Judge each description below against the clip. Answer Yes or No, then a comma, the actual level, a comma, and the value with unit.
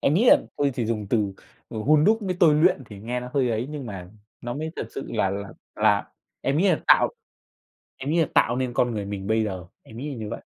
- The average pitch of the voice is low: Yes, low, 120 Hz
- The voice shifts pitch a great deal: Yes, wide, 5.7 semitones